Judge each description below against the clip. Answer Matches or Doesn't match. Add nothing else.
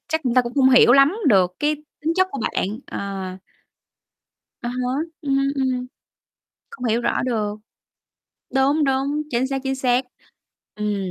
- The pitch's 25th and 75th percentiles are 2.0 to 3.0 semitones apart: Matches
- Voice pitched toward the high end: Matches